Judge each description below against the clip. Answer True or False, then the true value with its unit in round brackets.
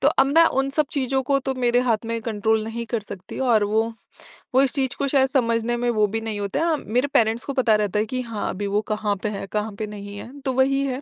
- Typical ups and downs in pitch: True (3.8 semitones)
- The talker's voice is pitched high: True (230 Hz)